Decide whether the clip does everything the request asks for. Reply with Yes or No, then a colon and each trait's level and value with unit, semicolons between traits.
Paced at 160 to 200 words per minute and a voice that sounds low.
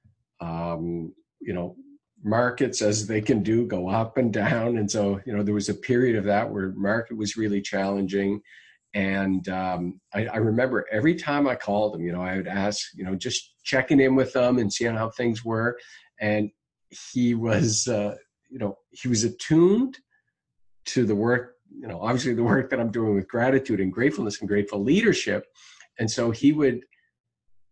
Yes: average, 185 wpm; low, 110 Hz